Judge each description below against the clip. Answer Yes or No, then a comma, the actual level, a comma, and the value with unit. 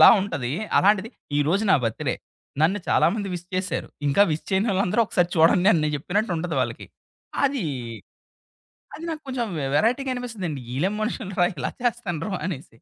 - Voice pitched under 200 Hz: Yes, high, 190 Hz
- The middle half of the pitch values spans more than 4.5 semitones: Yes, wide, 5.5 semitones